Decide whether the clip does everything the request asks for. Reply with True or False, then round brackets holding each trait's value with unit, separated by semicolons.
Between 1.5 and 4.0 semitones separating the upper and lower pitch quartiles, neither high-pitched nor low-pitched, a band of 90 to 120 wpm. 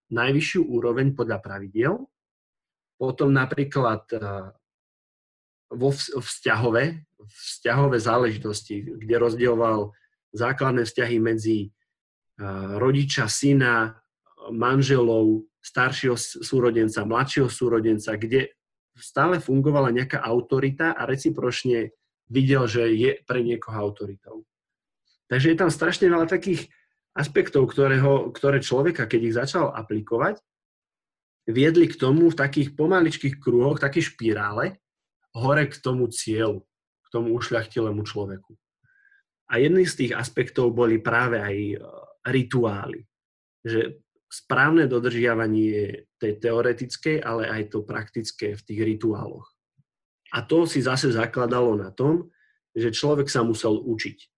False (3.7 semitones; 120 Hz; 110 wpm)